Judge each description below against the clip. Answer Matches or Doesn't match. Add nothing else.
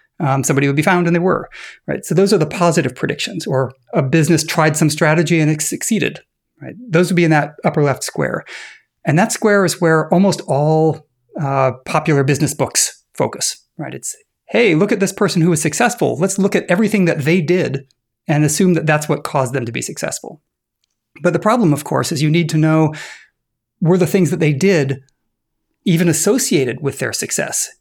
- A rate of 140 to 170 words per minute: Doesn't match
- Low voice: Doesn't match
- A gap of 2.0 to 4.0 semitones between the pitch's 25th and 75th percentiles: Matches